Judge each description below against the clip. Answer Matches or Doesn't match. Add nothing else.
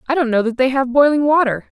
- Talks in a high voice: Matches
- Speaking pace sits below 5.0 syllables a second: Doesn't match